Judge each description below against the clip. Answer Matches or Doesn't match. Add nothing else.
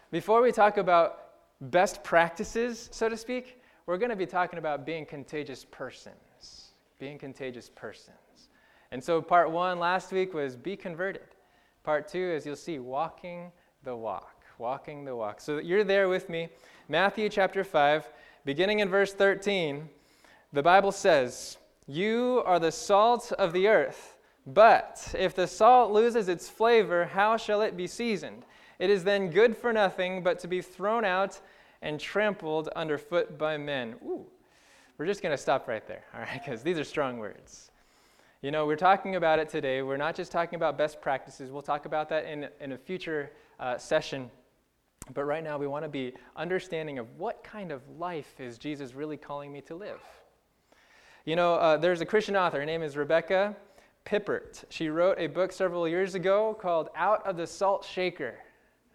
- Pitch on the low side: Doesn't match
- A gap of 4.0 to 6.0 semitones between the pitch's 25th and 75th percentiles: Matches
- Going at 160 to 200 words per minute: Matches